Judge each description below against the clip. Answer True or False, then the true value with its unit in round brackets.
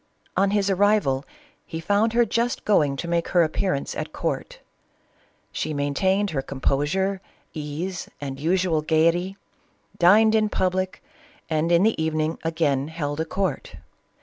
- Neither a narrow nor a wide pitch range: True (4.2 semitones)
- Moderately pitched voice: True (170 Hz)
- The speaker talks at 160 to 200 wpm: False (145 wpm)